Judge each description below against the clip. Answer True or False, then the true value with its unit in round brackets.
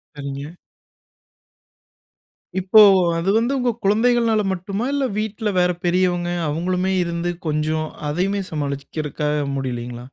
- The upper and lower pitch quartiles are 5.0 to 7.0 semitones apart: True (5.4 semitones)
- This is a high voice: False (175 Hz)